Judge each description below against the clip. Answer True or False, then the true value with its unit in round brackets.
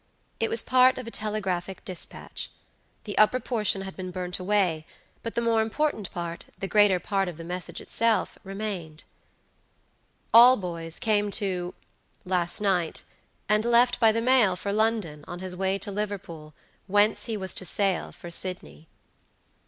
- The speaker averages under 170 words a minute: True (155 wpm)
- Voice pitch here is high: True (195 Hz)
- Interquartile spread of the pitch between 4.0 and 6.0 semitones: False (3.4 semitones)